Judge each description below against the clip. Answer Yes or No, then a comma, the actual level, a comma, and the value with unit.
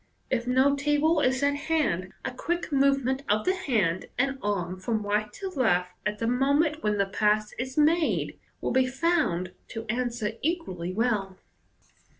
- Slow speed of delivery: No, average, 160 wpm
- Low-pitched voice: No, very high, 250 Hz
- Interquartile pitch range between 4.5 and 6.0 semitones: Yes, wide, 5.4 semitones